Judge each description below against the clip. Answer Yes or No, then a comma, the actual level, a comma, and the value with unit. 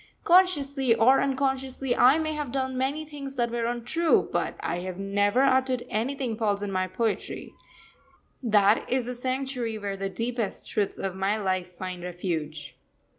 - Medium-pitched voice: No, high, 235 Hz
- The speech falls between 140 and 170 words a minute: Yes, average, 160 wpm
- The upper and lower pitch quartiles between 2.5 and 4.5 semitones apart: No, average, 5.2 semitones